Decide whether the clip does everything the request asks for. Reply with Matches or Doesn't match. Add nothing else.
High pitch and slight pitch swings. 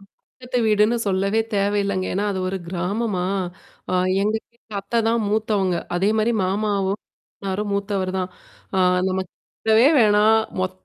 Matches